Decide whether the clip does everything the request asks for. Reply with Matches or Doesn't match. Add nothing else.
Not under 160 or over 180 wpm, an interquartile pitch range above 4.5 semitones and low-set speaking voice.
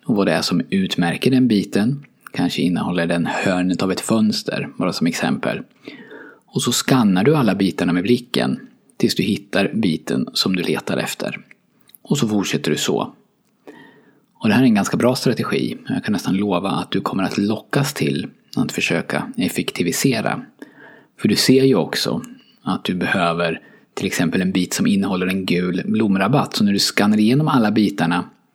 Matches